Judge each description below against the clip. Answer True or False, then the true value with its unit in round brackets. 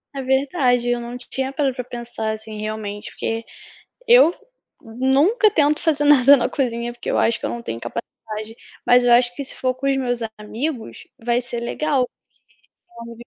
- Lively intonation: False (2.8 semitones)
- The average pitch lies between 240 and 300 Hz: True (245 Hz)